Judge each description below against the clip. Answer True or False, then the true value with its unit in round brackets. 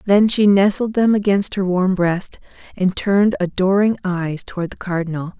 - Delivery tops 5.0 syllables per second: False (4.9 syllables/s)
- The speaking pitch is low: False (190 Hz)